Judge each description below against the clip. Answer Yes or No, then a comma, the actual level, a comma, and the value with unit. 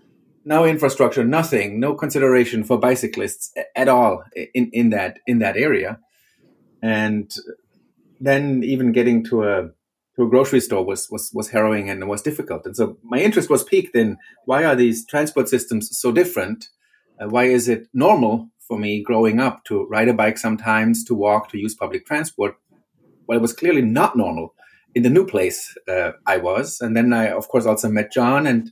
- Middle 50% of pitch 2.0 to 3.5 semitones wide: No, average, 3.9 semitones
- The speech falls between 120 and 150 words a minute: No, average, 185 wpm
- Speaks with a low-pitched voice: Yes, low, 120 Hz